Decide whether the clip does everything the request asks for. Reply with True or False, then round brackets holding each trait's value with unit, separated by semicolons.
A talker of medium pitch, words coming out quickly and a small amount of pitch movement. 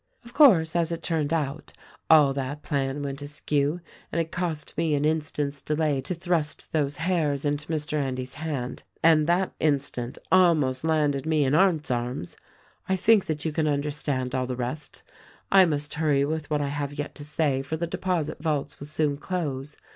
False (150 Hz; 185 wpm; 2.3 semitones)